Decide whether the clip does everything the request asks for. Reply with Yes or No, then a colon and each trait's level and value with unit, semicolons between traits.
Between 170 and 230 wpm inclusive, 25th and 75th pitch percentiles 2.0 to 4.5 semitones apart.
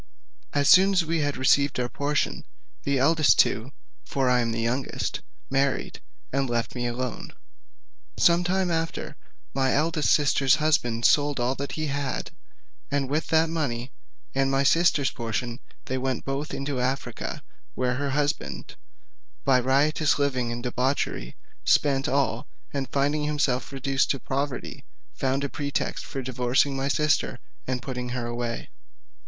No: average, 150 wpm; narrow, 2.4 semitones